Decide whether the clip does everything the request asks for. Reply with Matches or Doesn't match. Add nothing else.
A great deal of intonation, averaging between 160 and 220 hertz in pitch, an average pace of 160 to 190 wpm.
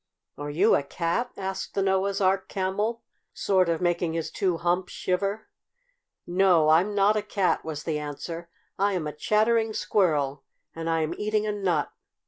Doesn't match